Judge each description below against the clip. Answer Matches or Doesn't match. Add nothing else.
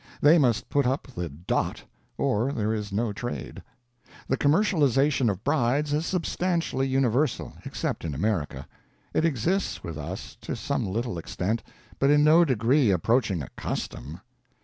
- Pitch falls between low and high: Doesn't match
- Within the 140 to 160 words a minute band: Matches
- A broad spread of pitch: Matches